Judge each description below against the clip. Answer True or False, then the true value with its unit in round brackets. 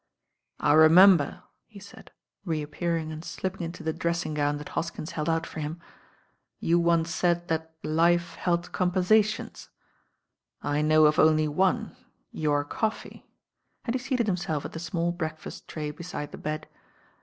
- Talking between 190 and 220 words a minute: False (155 wpm)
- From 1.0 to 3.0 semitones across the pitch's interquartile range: True (2.4 semitones)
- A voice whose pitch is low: False (165 Hz)